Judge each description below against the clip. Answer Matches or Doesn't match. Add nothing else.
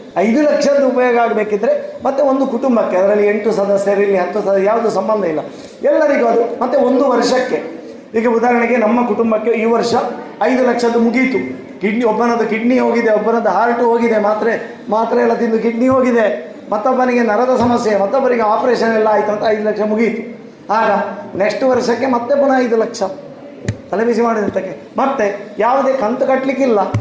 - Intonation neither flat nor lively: Matches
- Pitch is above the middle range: Matches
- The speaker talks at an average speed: Doesn't match